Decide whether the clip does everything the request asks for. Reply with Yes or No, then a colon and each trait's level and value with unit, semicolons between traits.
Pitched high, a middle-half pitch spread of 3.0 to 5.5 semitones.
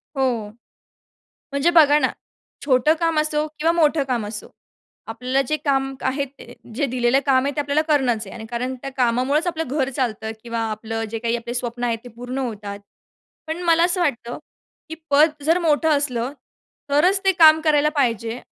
Yes: very high, 270 Hz; average, 4.2 semitones